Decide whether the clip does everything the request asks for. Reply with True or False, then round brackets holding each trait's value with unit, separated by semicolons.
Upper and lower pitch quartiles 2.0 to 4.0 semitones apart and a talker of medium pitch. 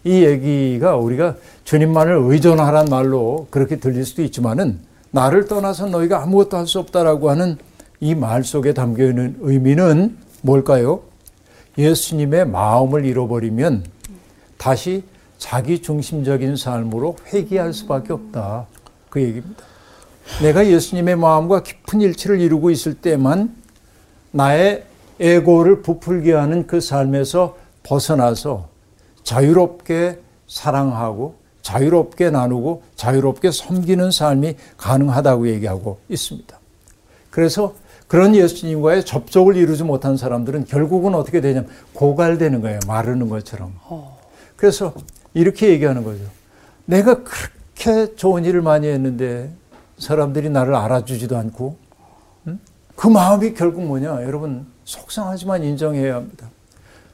False (5.7 semitones; 145 Hz)